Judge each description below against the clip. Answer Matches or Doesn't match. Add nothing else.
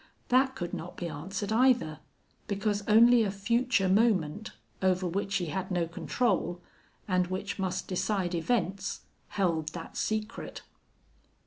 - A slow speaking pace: Matches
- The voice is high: Matches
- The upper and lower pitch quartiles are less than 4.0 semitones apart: Matches